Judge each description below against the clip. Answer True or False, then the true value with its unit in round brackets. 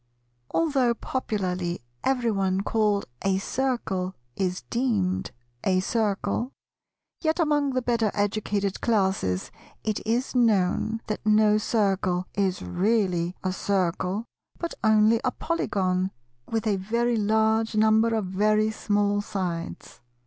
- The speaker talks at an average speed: False (115 wpm)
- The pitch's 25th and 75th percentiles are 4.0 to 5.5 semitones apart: False (3.3 semitones)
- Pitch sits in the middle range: False (210 Hz)